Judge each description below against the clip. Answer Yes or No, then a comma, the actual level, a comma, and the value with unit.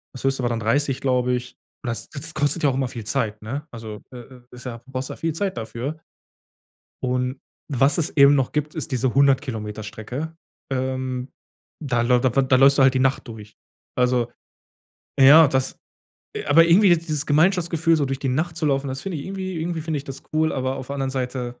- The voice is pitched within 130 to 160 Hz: Yes, low, 135 Hz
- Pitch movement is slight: No, average, 3.3 semitones